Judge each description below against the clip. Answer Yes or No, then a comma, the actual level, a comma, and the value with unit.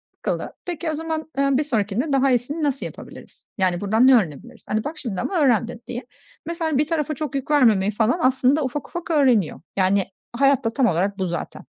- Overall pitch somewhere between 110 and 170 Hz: No, very high, 260 Hz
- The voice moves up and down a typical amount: No, wide, 5.8 semitones